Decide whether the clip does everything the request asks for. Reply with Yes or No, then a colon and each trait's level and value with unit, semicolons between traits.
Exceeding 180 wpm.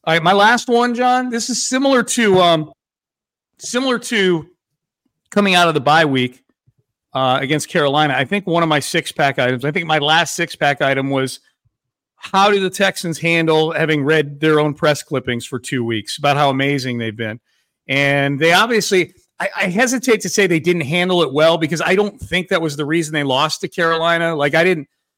Yes: fast, 205 wpm